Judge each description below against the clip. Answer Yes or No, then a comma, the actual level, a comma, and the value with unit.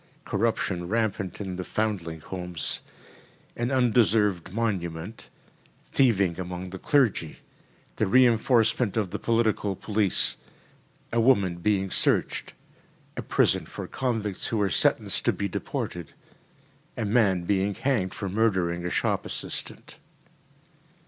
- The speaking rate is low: Yes, slow, 120 wpm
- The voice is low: Yes, low, 100 Hz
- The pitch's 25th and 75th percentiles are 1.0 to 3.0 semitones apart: No, average, 3.8 semitones